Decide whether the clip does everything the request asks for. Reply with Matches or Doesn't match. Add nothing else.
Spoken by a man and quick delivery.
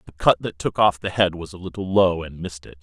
Matches